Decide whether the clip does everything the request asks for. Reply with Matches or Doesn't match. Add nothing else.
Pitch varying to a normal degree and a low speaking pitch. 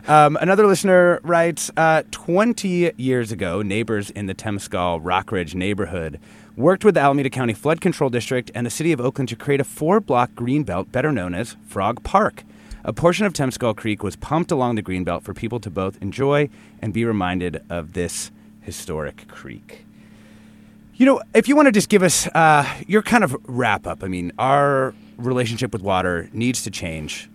Doesn't match